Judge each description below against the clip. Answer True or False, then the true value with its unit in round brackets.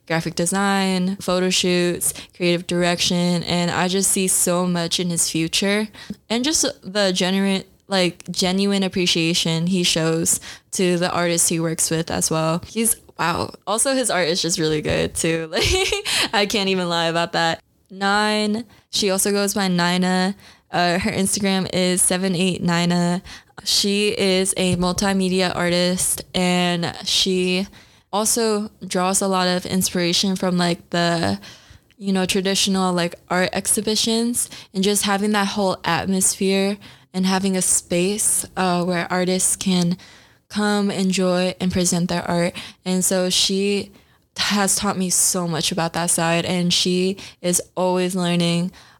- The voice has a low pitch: False (185 Hz)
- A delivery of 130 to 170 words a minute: True (145 wpm)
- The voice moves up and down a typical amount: False (1.9 semitones)